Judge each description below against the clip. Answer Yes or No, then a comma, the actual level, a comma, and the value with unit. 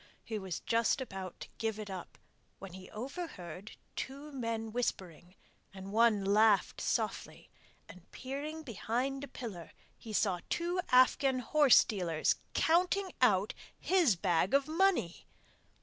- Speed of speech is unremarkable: No, slow, 130 wpm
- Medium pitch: No, high, 225 Hz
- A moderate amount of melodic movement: No, wide, 6.3 semitones